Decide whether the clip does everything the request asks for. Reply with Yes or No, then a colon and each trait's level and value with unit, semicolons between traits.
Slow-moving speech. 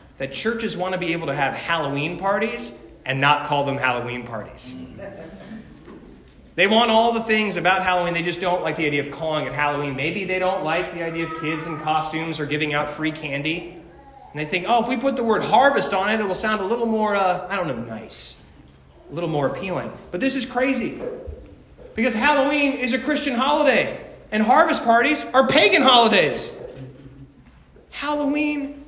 No: average, 190 wpm